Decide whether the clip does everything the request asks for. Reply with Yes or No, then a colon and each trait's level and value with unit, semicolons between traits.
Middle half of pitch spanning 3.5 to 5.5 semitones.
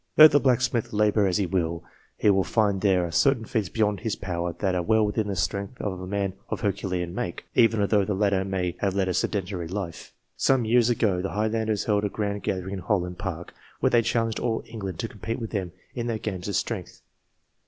No: average, 3.0 semitones